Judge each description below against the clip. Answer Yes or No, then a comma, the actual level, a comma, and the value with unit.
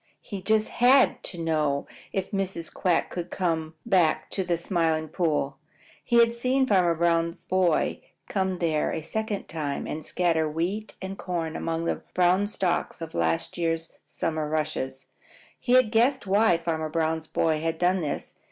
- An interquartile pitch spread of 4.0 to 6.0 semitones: No, average, 3.5 semitones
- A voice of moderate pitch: Yes, medium, 170 Hz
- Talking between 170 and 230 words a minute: No, average, 160 wpm